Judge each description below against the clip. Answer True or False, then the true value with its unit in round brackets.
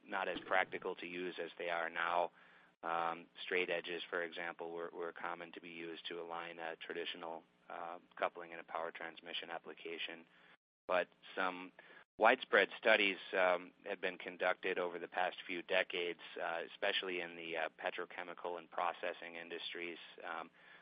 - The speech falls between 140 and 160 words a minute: True (155 wpm)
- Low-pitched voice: True (85 Hz)